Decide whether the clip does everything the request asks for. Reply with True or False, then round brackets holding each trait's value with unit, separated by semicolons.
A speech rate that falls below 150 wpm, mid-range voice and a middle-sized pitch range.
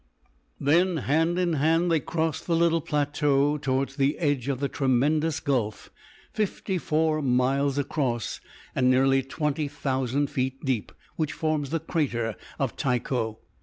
True (140 wpm; 145 Hz; 3.1 semitones)